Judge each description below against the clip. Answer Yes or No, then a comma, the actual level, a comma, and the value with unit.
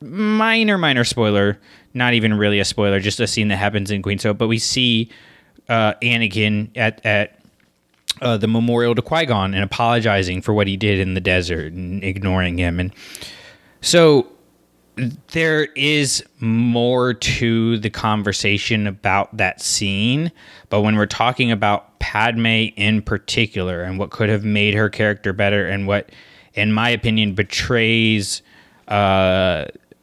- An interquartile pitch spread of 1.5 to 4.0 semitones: Yes, average, 2.9 semitones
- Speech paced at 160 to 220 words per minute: No, average, 150 wpm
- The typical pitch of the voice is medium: No, low, 105 Hz